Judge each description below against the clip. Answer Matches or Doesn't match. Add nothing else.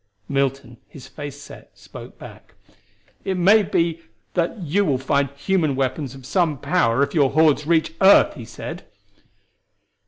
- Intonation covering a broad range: Doesn't match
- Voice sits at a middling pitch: Matches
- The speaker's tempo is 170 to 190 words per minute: Doesn't match